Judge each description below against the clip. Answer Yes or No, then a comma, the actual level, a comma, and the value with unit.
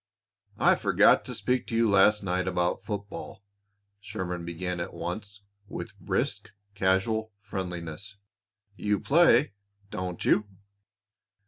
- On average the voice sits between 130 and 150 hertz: No, low, 100 Hz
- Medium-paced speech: No, slow, 115 wpm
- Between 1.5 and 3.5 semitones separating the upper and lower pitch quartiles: Yes, average, 2.9 semitones